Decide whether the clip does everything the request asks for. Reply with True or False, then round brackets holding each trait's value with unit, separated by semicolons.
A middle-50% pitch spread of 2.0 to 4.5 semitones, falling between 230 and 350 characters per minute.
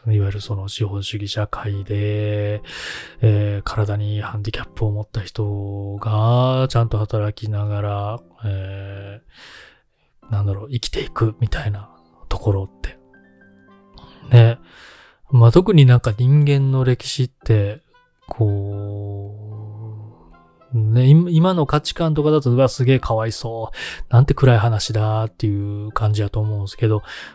True (2.7 semitones; 265 characters per minute)